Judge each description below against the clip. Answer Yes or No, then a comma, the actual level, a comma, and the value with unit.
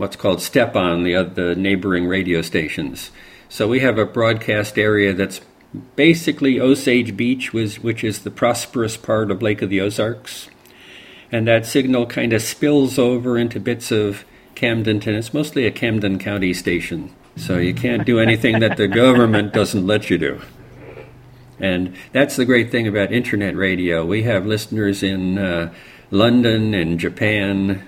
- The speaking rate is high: No, average, 165 wpm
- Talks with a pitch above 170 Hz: No, low, 110 Hz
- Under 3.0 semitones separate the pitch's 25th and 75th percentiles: No, average, 3.6 semitones